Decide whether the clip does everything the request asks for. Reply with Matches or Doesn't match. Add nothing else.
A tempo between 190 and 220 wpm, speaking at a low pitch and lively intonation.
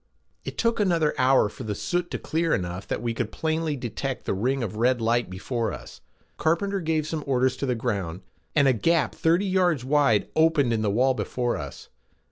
Matches